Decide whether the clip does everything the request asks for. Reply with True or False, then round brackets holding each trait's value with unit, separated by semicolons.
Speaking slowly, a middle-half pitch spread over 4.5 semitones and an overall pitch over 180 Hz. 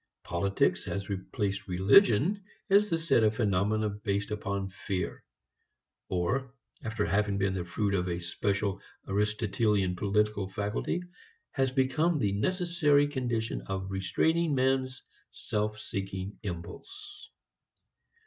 False (115 wpm; 5.2 semitones; 105 Hz)